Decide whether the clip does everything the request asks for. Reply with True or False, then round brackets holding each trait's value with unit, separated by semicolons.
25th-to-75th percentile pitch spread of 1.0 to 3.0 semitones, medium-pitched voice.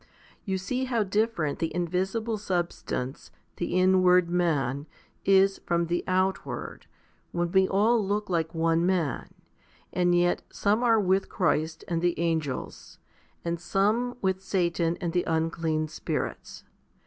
True (2.7 semitones; 180 Hz)